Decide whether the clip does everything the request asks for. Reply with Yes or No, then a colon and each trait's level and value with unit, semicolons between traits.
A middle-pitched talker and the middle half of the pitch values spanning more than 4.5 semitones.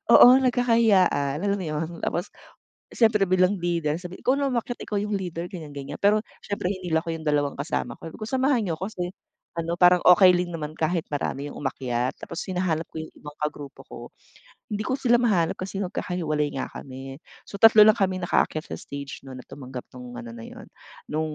Yes: medium, 175 Hz; average, 5.3 semitones